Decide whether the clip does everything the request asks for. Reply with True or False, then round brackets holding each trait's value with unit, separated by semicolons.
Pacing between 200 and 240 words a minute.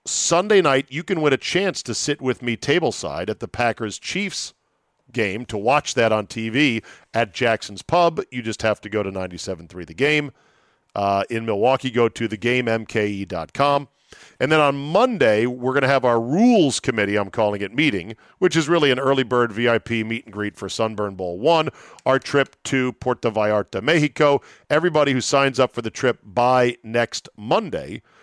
False (180 wpm)